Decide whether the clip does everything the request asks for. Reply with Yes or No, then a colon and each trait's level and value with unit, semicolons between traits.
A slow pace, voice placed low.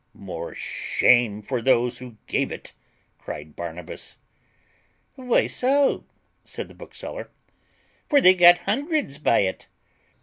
Yes: slow, 115 wpm; low, 130 Hz